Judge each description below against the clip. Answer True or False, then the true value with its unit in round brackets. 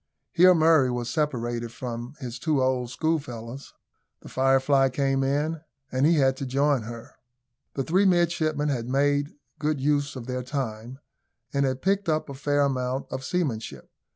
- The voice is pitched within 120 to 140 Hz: True (135 Hz)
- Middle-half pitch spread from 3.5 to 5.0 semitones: False (2.8 semitones)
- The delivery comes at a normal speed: True (160 wpm)